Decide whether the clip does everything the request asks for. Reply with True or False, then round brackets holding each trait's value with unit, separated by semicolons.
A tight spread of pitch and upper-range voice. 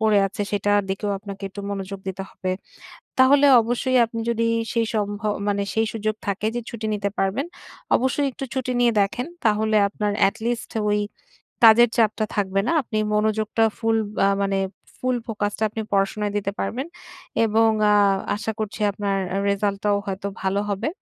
True (2.1 semitones; 210 Hz)